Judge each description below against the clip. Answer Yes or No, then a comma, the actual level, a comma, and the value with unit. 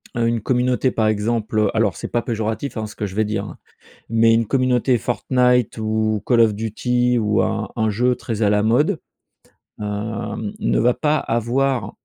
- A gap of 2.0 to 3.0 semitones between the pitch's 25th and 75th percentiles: Yes, narrow, 2.4 semitones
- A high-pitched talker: No, low, 115 Hz